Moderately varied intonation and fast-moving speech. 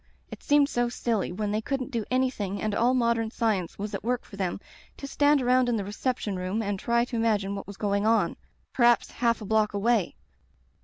Yes: average, 3.2 semitones; fast, 215 wpm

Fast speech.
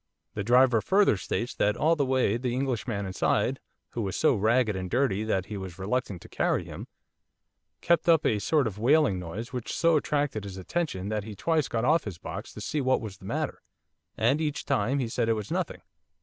Yes: fast, 210 wpm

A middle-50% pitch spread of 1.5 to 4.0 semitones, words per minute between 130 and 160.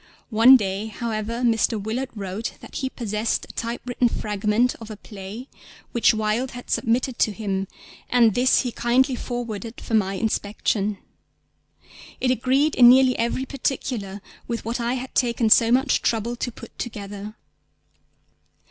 Yes: average, 2.7 semitones; average, 150 wpm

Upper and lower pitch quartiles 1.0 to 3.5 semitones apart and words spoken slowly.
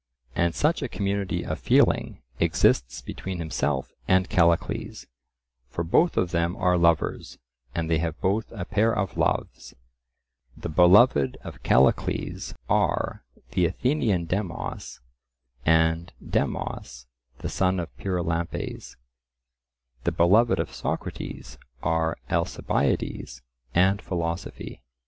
Yes: average, 2.9 semitones; slow, 110 wpm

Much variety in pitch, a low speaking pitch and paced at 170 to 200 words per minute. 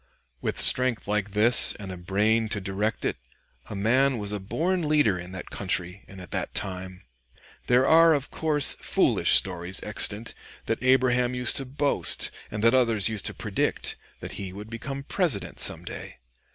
No: average, 4.8 semitones; low, 110 Hz; average, 175 wpm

